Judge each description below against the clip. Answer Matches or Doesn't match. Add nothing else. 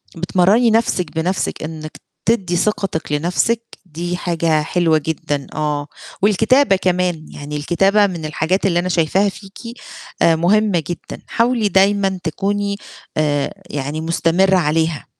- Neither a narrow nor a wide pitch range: Matches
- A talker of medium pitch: Matches